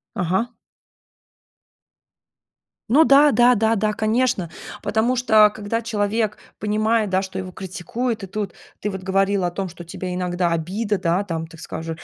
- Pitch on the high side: Yes, high, 205 Hz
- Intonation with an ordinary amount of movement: Yes, average, 3.5 semitones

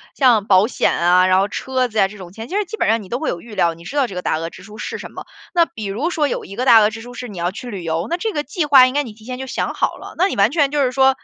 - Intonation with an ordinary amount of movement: No, wide, 5.8 semitones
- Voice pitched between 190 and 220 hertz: No, high, 230 Hz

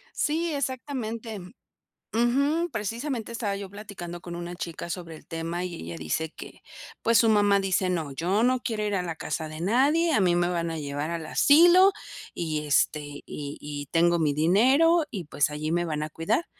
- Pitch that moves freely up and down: Yes, wide, 6.4 semitones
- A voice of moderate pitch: Yes, medium, 180 Hz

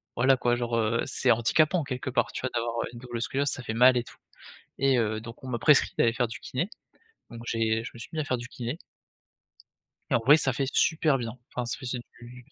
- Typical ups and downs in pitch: No, narrow, 2.3 semitones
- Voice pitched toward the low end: Yes, low, 125 Hz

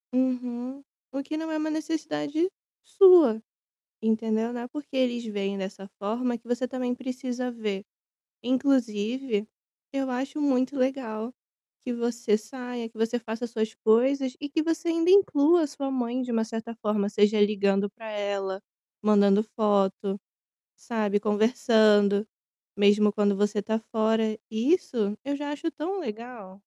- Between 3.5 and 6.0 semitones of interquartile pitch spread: Yes, average, 4.0 semitones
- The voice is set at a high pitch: Yes, high, 235 Hz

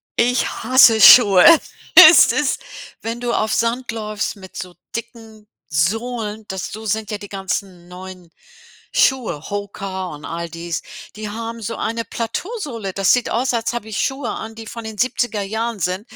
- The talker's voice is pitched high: Yes, high, 220 Hz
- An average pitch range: Yes, average, 3.3 semitones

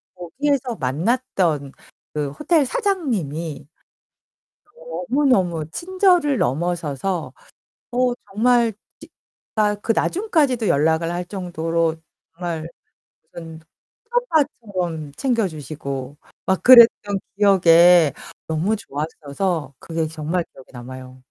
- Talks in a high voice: No, medium, 175 Hz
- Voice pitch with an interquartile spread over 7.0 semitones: Yes, wide, 7.8 semitones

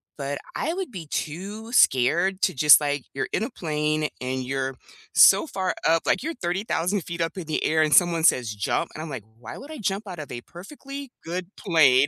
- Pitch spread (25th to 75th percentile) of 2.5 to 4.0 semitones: No, average, 5.3 semitones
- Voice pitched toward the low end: No, medium, 165 Hz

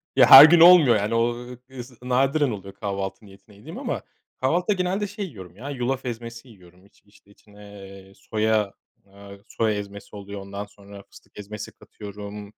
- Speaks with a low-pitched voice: Yes, low, 105 Hz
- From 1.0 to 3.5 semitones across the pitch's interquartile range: No, average, 4.2 semitones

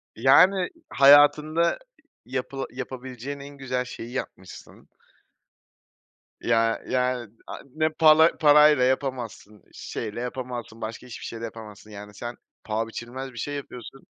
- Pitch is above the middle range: No, low, 125 Hz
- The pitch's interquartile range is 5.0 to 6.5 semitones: No, average, 3.7 semitones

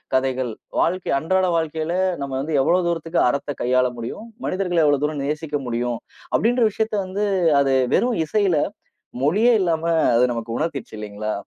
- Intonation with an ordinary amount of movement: No, wide, 5.9 semitones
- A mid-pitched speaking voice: Yes, medium, 155 Hz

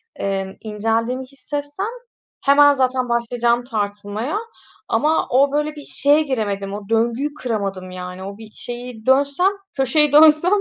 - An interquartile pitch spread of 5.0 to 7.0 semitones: Yes, average, 5.3 semitones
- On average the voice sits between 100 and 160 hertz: No, high, 245 Hz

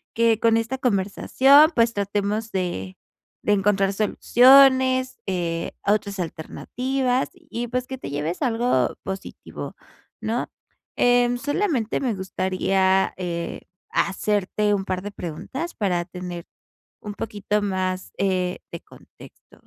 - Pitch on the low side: No, high, 205 Hz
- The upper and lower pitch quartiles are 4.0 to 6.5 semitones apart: Yes, average, 4.7 semitones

